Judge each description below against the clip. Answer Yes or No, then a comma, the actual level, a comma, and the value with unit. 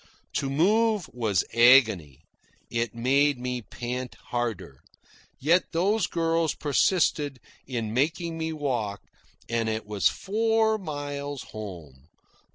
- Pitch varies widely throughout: Yes, wide, 6.3 semitones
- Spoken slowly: Yes, slow, 110 wpm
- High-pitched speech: No, low, 135 Hz